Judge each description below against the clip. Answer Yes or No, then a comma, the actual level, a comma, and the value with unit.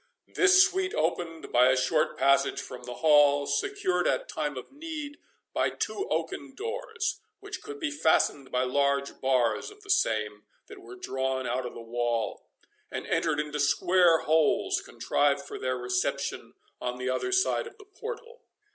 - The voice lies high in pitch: No, medium, 150 Hz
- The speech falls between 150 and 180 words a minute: Yes, average, 165 wpm